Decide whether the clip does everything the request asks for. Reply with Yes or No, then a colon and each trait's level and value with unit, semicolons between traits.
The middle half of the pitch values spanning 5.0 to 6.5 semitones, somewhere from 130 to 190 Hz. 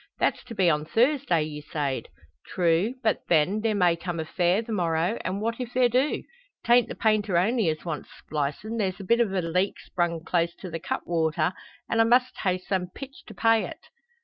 Yes: average, 5.3 semitones; medium, 185 Hz